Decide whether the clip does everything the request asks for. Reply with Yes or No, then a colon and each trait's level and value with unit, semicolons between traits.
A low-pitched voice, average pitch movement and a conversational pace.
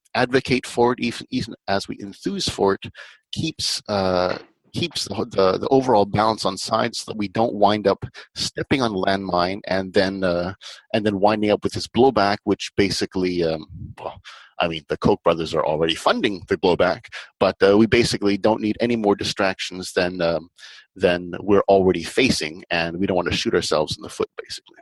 Yes: low, 100 Hz; average, 3.3 semitones; average, 190 wpm